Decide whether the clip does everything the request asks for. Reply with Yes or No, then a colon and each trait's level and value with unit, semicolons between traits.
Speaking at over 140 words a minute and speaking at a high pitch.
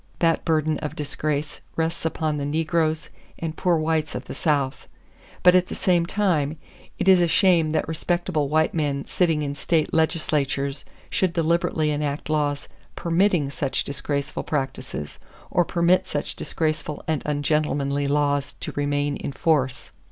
No: average, 150 wpm; medium, 155 Hz